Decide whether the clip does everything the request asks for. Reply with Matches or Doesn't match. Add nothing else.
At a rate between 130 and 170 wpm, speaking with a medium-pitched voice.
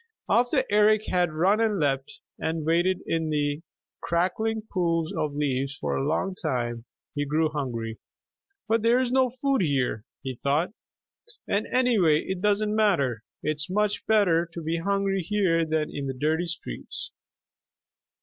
Matches